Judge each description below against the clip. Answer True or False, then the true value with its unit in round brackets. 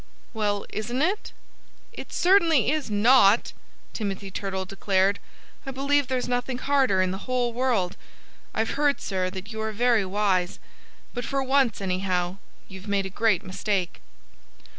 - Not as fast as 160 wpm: True (145 wpm)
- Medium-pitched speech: False (215 Hz)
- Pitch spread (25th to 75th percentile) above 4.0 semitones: True (5.1 semitones)